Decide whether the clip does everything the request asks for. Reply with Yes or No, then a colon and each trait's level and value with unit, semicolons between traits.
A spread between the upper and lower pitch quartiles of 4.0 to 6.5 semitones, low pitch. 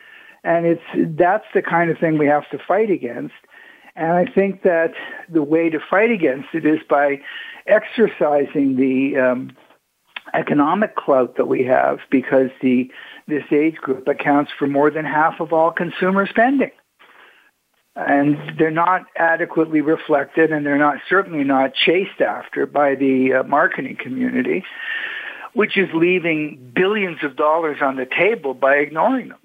No: average, 4.6 semitones; medium, 160 Hz